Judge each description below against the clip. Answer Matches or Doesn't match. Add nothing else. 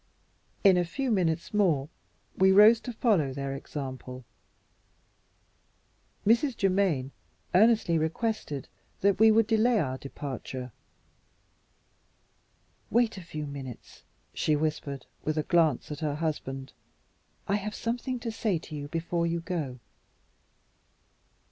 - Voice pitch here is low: Doesn't match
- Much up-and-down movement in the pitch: Matches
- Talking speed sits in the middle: Doesn't match